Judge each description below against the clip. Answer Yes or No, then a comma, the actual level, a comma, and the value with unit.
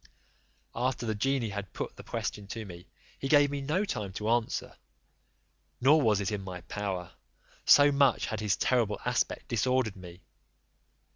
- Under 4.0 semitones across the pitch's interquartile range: No, average, 5.3 semitones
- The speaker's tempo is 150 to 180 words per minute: Yes, average, 160 wpm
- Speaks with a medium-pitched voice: No, low, 110 Hz